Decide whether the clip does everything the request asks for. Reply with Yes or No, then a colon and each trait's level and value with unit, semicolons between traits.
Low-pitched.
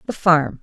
No: medium, 155 Hz